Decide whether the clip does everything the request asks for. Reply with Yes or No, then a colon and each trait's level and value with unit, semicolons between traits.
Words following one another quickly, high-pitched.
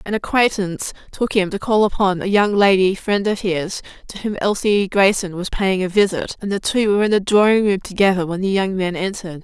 Yes: fast, 225 wpm; high, 195 Hz